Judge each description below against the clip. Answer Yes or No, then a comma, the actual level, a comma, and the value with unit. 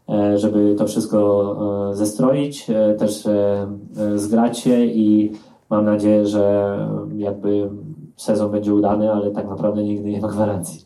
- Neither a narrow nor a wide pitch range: No, narrow, 0.7 semitones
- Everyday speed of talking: Yes, average, 120 wpm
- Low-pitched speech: Yes, low, 105 Hz